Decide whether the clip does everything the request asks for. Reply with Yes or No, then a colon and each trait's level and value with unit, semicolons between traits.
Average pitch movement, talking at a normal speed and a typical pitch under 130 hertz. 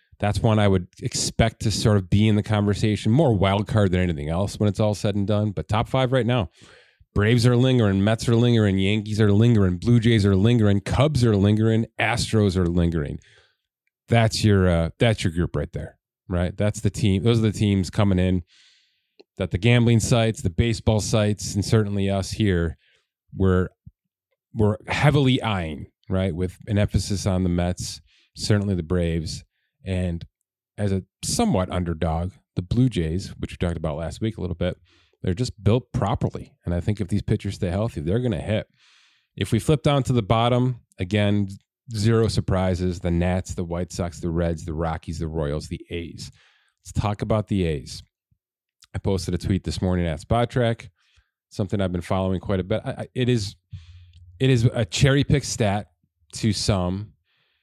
Yes: average, 3.8 semitones; average, 185 wpm; low, 100 Hz